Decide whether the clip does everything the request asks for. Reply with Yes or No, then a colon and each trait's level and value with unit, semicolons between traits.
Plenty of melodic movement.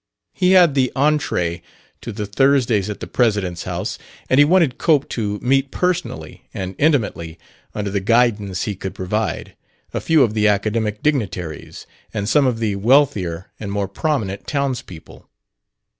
Yes: wide, 5.8 semitones